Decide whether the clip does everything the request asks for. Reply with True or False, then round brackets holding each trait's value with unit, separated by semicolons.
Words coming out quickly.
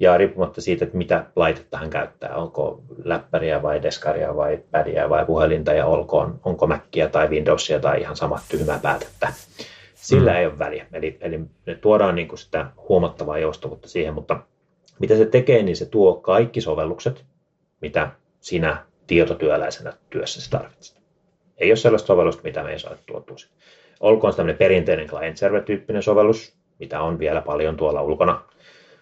True (160 wpm)